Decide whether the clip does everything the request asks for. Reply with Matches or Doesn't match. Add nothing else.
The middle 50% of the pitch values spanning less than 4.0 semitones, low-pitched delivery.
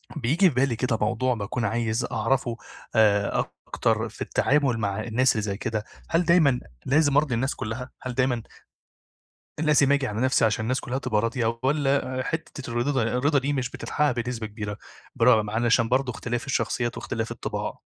Matches